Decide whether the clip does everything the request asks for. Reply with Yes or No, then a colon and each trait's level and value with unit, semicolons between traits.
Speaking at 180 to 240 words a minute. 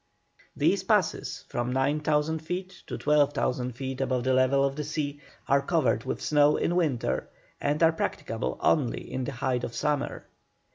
No: average, 160 wpm